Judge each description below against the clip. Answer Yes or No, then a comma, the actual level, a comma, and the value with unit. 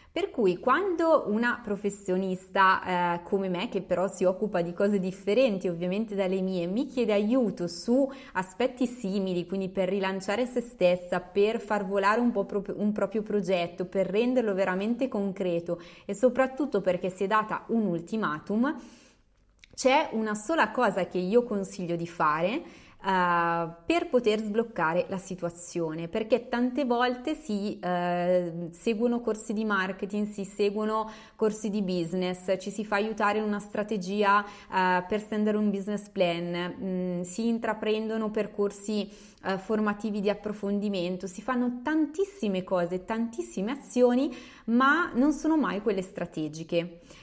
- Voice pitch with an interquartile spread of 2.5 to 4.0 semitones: Yes, average, 3.7 semitones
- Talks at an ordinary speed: Yes, average, 140 wpm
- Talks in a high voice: Yes, high, 205 Hz